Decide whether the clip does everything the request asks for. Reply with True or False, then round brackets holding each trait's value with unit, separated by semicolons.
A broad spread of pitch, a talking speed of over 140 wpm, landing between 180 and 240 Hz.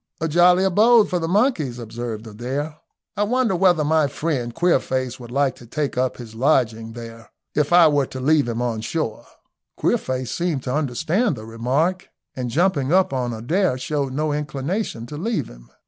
False (6.0 semitones; 180 wpm; 140 Hz)